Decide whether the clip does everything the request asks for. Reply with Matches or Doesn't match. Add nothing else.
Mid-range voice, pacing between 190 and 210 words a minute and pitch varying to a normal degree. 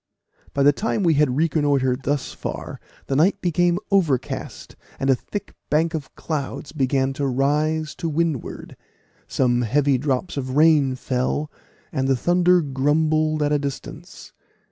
Doesn't match